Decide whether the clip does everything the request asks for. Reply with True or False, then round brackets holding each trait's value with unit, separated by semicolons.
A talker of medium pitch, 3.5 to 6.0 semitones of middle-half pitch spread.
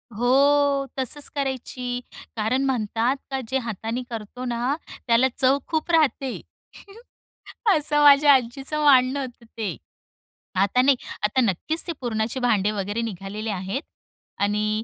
False (250 Hz; 3.9 semitones)